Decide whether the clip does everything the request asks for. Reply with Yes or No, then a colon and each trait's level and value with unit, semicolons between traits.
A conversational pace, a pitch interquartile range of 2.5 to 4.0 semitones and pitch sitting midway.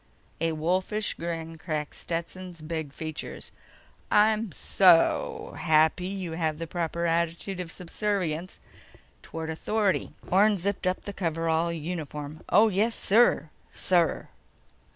No: slow, 115 wpm; average, 2.8 semitones; medium, 170 Hz